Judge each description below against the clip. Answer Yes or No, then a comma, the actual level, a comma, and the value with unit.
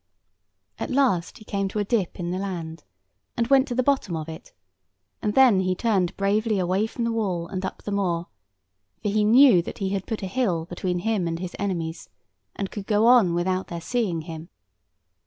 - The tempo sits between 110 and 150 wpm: No, fast, 205 wpm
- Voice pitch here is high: Yes, high, 195 Hz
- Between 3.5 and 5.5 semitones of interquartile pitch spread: Yes, average, 4.1 semitones